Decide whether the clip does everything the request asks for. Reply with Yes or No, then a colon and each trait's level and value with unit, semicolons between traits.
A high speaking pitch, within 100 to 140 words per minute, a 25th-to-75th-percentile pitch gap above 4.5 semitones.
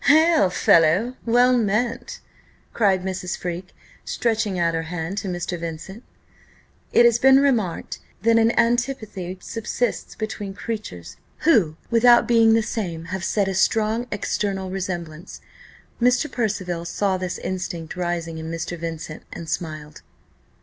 Yes: high, 195 Hz; slow, 135 wpm; average, 5.1 semitones